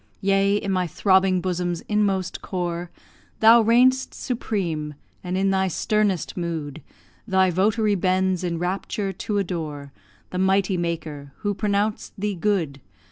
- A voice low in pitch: No, high, 190 Hz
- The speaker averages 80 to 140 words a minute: Yes, slow, 135 wpm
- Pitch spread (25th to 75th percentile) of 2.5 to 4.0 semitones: Yes, average, 2.8 semitones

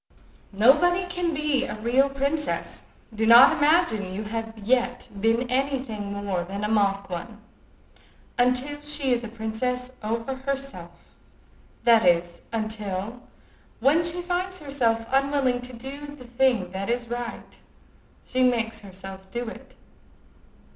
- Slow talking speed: Yes, slow, 130 wpm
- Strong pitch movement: No, average, 4.3 semitones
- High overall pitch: Yes, high, 240 Hz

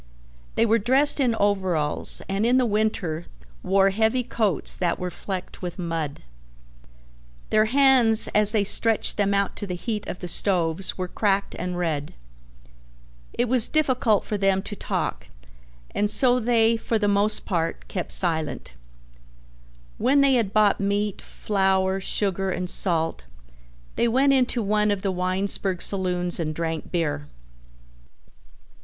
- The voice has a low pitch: No, high, 200 Hz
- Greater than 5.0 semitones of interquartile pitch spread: No, average, 3.7 semitones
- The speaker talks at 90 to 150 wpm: Yes, average, 145 wpm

